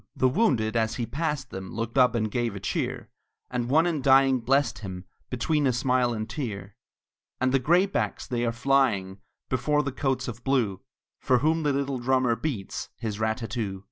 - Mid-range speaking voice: No, low, 125 Hz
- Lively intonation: No, average, 3.6 semitones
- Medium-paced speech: Yes, average, 190 wpm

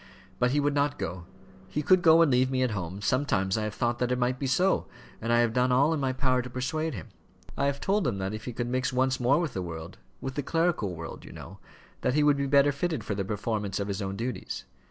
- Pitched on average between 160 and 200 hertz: No, low, 125 Hz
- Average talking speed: No, fast, 265 wpm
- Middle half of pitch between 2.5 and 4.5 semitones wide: No, average, 5.1 semitones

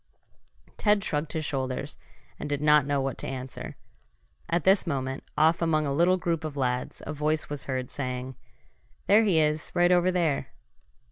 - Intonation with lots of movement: No, average, 3.9 semitones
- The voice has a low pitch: No, medium, 150 Hz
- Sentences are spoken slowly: No, average, 175 wpm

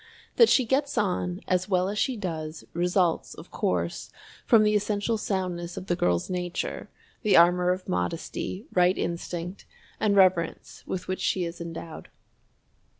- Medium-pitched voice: Yes, medium, 180 Hz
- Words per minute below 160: Yes, average, 150 wpm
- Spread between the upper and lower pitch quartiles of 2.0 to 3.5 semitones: Yes, average, 2.9 semitones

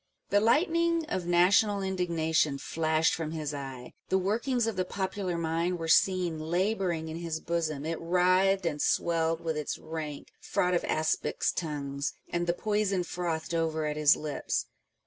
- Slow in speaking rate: No, average, 165 wpm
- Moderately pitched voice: Yes, medium, 170 Hz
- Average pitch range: Yes, average, 3.0 semitones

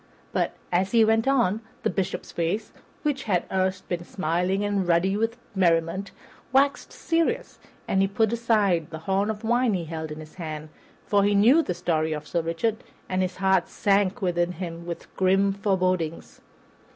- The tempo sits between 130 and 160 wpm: No, average, 175 wpm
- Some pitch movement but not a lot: Yes, average, 3.7 semitones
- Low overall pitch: No, high, 190 Hz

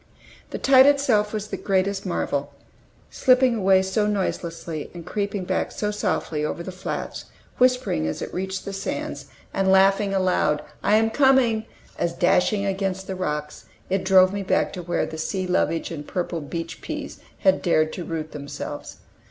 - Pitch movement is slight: No, average, 3.4 semitones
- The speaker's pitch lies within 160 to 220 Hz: Yes, high, 190 Hz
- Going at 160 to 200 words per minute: Yes, average, 170 wpm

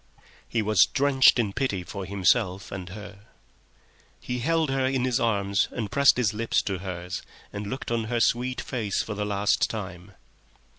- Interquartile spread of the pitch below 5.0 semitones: Yes, average, 4.0 semitones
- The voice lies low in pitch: Yes, low, 105 Hz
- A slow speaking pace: No, average, 170 wpm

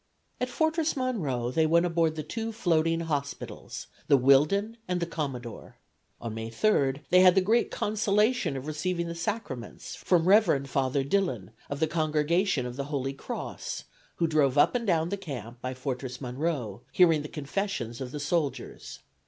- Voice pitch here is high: No, medium, 155 Hz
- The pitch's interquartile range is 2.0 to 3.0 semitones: No, wide, 5.5 semitones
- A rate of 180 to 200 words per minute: No, average, 170 wpm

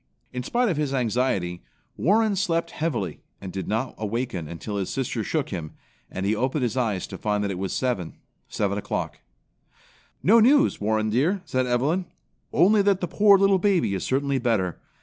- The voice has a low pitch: Yes, low, 125 Hz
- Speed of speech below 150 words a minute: No, average, 180 wpm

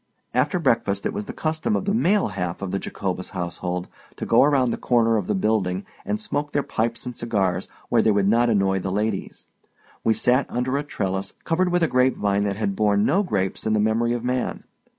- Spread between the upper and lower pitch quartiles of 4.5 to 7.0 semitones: Yes, average, 4.8 semitones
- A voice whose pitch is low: Yes, low, 110 Hz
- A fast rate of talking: Yes, fast, 215 wpm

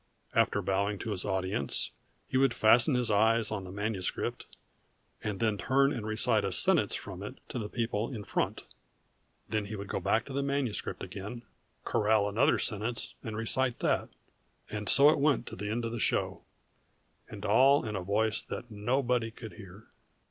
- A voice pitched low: Yes, low, 110 Hz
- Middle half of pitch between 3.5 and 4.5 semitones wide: No, average, 3.0 semitones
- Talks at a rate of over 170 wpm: Yes, average, 180 wpm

